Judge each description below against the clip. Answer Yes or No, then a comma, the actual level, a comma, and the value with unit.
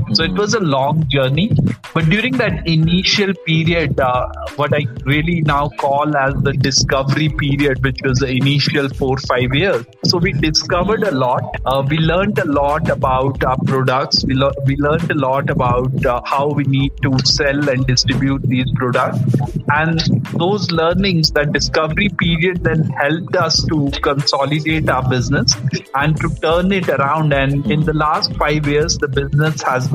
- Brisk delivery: No, average, 170 wpm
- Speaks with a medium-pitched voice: Yes, medium, 145 Hz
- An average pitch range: Yes, average, 3.1 semitones